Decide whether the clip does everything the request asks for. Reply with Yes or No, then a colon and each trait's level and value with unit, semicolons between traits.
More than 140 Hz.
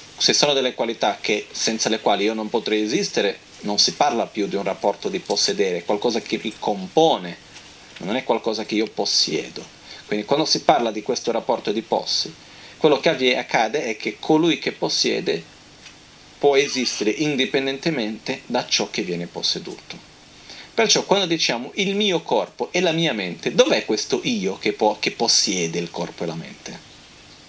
No: low, 135 Hz